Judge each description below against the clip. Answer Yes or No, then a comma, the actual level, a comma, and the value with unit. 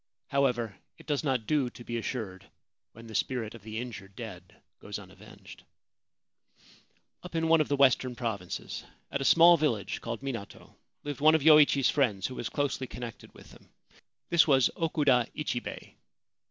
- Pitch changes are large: No, average, 4.2 semitones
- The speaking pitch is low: Yes, low, 125 Hz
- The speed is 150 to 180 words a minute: Yes, average, 165 wpm